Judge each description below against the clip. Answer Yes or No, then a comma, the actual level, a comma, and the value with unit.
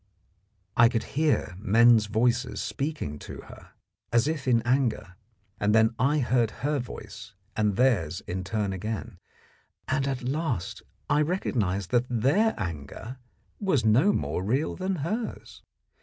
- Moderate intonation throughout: Yes, average, 5.0 semitones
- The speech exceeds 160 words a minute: No, average, 140 wpm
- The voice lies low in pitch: Yes, low, 120 Hz